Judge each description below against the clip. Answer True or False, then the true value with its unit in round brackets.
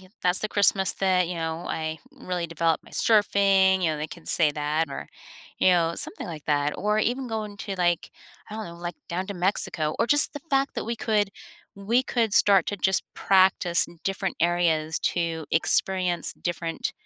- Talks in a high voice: False (180 Hz)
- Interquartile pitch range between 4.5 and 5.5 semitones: False (3.5 semitones)